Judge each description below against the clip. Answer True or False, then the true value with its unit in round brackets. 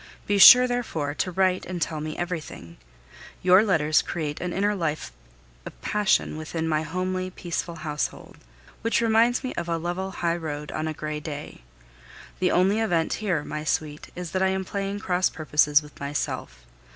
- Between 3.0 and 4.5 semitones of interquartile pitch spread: True (3.8 semitones)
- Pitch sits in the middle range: True (170 Hz)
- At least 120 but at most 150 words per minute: False (170 wpm)